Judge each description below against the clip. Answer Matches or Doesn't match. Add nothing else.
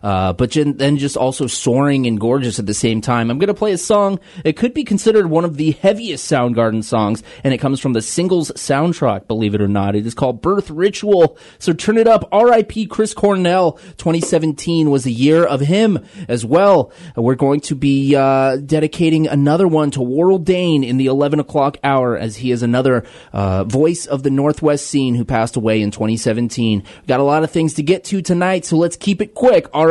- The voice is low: Doesn't match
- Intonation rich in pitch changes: Matches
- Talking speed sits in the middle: Doesn't match